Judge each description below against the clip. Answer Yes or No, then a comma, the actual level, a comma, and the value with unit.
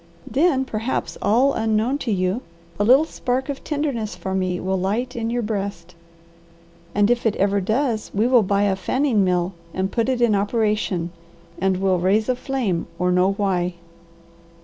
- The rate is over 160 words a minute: Yes, average, 170 wpm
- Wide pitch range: No, average, 4.4 semitones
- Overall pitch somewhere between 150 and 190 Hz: No, high, 210 Hz